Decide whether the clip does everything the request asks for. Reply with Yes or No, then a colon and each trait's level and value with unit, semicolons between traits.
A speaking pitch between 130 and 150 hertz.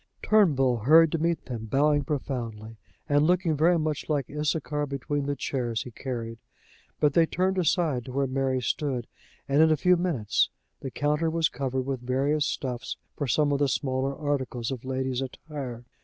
Yes: medium, 140 Hz